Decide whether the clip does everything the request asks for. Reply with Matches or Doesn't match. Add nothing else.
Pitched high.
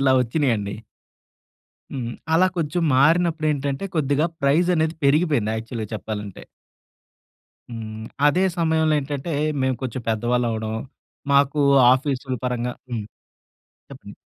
Doesn't match